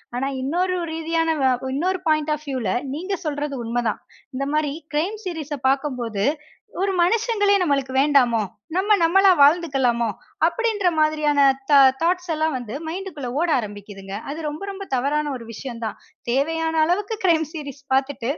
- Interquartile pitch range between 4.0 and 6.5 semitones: Yes, average, 4.6 semitones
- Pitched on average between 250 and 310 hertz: Yes, very high, 300 Hz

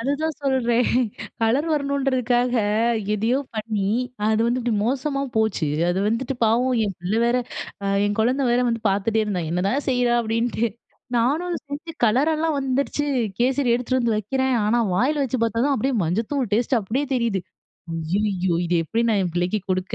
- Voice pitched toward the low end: No, high, 235 Hz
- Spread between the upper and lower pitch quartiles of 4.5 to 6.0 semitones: No, average, 3.9 semitones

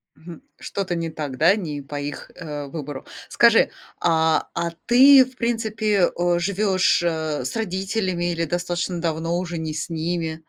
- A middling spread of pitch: Yes, average, 3.2 semitones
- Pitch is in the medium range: Yes, medium, 170 Hz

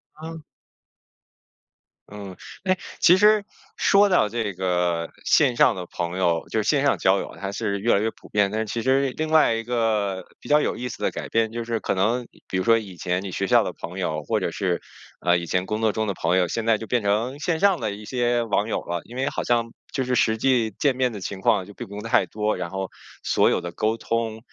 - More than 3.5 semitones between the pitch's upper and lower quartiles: Yes, average, 4.2 semitones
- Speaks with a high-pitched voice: No, low, 110 Hz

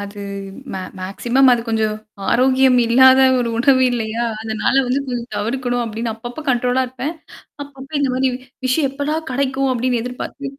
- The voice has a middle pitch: No, very high, 250 Hz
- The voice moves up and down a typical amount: No, narrow, 2.2 semitones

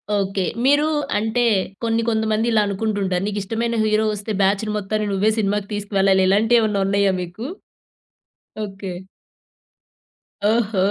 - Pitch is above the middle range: Yes, high, 210 Hz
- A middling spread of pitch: No, narrow, 2.0 semitones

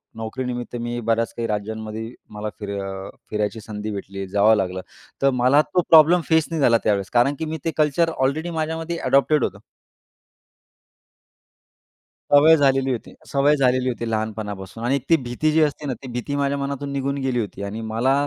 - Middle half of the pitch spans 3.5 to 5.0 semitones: Yes, average, 4.7 semitones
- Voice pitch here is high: No, low, 125 Hz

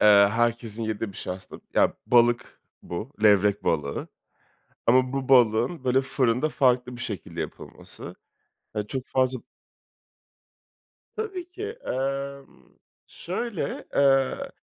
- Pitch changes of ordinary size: Yes, average, 3.9 semitones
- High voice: No, low, 125 Hz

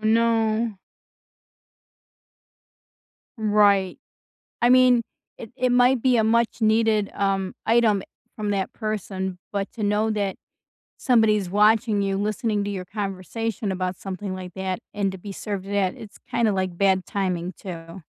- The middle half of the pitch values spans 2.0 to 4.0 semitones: Yes, average, 2.7 semitones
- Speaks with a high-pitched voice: Yes, high, 205 Hz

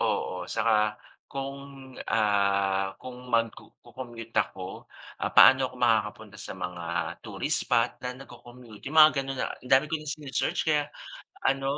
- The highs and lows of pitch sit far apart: No, average, 3.6 semitones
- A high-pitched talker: No, low, 125 Hz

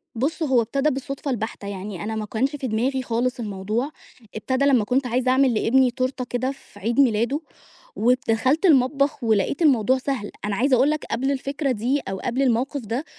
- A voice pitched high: Yes, very high, 255 Hz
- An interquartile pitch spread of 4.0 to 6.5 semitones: No, average, 3.4 semitones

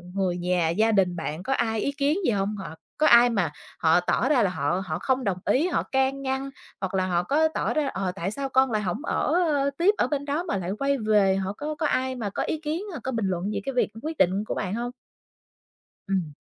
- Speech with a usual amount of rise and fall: No, wide, 6.8 semitones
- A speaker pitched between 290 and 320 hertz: No, high, 225 Hz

